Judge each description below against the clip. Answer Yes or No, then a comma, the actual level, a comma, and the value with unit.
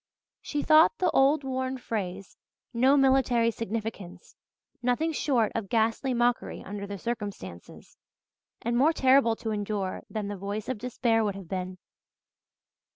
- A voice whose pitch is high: Yes, high, 230 Hz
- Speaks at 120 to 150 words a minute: Yes, average, 140 wpm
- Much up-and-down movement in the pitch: No, average, 4.3 semitones